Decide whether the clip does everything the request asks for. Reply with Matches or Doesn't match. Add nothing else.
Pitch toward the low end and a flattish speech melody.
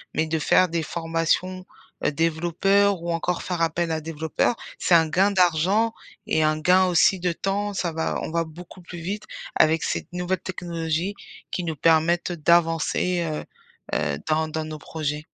Doesn't match